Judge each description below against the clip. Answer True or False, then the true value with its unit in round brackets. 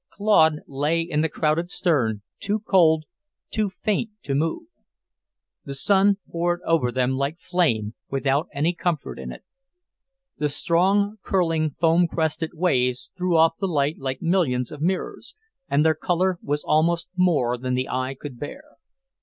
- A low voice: False (160 Hz)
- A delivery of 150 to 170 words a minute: True (155 wpm)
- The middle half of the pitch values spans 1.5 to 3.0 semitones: False (4.4 semitones)